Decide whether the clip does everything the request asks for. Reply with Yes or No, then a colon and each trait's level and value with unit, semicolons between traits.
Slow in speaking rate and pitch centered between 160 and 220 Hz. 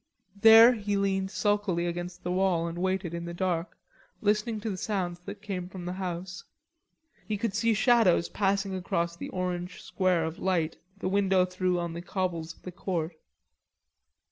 No: average, 170 wpm; medium, 185 Hz